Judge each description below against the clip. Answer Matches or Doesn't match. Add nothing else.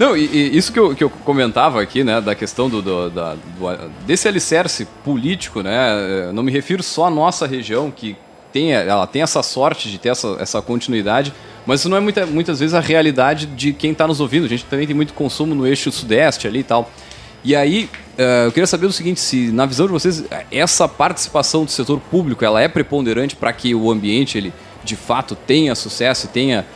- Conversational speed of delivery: Doesn't match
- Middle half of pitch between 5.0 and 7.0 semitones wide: Matches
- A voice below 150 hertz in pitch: Matches